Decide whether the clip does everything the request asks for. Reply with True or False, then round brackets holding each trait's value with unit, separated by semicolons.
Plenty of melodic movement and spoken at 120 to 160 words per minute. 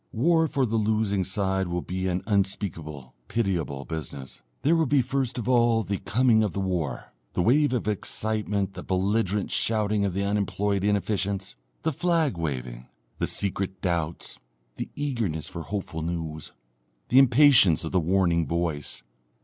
False (4.7 semitones; 155 wpm)